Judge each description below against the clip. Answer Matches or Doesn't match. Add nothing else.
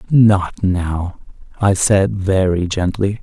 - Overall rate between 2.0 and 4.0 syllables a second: Matches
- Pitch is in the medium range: Doesn't match